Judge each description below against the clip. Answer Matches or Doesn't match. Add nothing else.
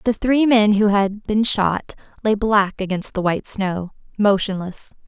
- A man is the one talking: Doesn't match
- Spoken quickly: Doesn't match